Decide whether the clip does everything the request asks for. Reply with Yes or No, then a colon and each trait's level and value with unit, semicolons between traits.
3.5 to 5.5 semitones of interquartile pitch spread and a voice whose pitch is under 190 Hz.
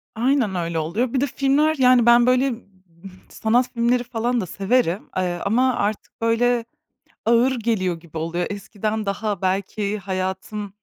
No: average, 4.5 semitones; high, 220 Hz